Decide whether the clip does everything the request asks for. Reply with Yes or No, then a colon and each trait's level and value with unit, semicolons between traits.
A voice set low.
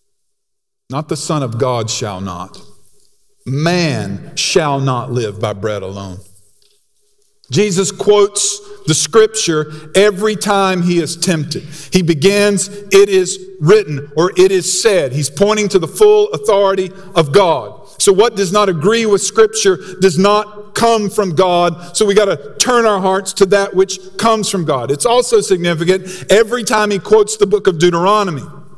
No: high, 195 Hz